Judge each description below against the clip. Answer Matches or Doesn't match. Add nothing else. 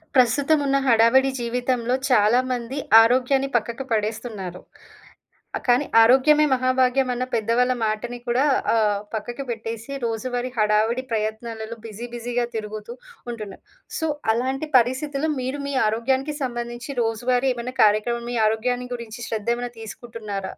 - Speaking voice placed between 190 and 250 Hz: Matches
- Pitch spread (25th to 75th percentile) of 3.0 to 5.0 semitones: Doesn't match